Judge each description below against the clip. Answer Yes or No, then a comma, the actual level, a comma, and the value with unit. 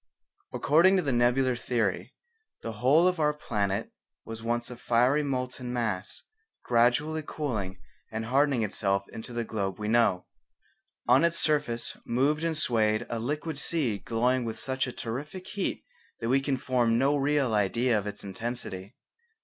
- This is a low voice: Yes, low, 120 Hz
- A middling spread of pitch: Yes, average, 4.1 semitones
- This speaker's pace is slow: No, average, 155 wpm